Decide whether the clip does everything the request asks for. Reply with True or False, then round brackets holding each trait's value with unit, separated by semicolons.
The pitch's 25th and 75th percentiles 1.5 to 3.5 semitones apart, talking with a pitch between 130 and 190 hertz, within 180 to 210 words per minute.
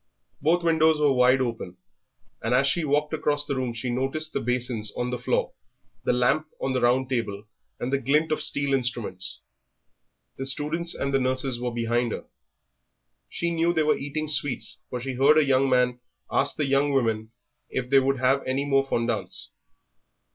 True (2.9 semitones; 135 Hz; 185 wpm)